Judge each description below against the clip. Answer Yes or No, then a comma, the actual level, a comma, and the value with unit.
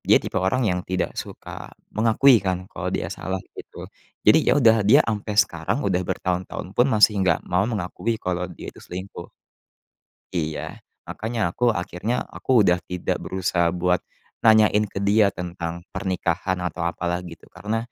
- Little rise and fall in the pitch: No, average, 3.4 semitones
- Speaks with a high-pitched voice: No, very low, 95 Hz